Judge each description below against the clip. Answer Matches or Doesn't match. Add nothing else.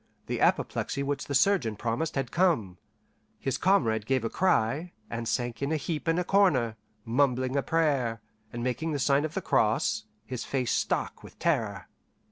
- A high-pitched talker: Doesn't match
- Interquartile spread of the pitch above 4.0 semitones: Matches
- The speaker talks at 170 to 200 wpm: Matches